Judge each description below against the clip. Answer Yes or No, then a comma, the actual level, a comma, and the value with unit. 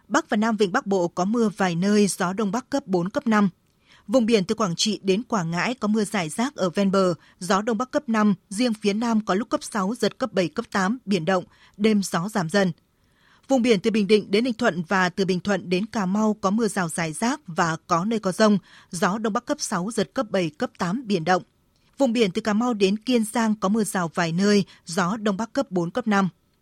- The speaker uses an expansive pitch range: No, average, 3.3 semitones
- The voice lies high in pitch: Yes, high, 205 Hz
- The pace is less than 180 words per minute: No, fast, 250 wpm